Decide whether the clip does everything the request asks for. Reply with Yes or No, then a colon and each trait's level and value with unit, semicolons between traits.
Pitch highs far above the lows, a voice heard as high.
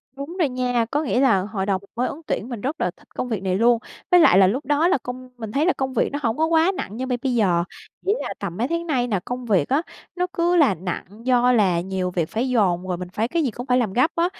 Yes: wide, 6.3 semitones; high, 245 Hz